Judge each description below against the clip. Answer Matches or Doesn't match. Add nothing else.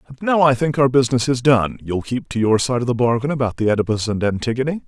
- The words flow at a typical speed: Doesn't match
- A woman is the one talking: Doesn't match